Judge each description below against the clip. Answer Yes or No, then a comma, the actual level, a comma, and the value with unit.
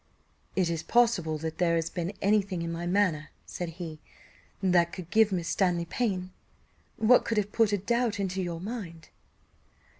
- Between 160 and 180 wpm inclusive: Yes, average, 175 wpm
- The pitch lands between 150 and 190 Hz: Yes, medium, 185 Hz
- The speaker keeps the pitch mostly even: No, average, 3.7 semitones